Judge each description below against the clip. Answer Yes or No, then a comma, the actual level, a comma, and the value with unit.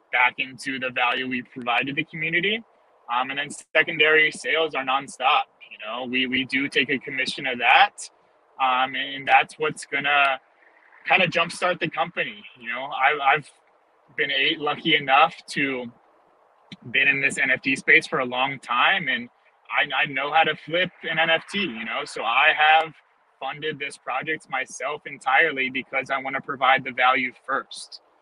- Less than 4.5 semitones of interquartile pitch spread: Yes, average, 3.5 semitones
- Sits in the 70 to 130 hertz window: No, medium, 140 Hz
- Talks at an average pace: Yes, average, 170 wpm